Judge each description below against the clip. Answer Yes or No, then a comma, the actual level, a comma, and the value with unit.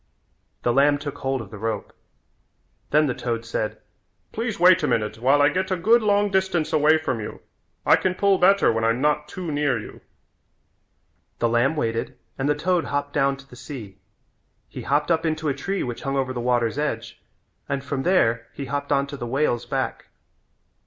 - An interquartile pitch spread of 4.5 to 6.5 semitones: Yes, average, 4.9 semitones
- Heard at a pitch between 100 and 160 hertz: Yes, medium, 140 Hz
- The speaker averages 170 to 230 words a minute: Yes, average, 195 wpm